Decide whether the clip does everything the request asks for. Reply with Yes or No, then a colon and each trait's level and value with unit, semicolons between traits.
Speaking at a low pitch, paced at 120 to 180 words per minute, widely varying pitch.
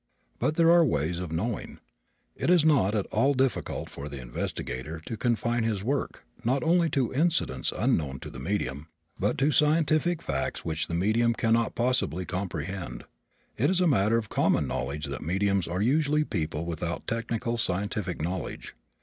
Yes: low, 105 Hz; average, 170 wpm; wide, 8.4 semitones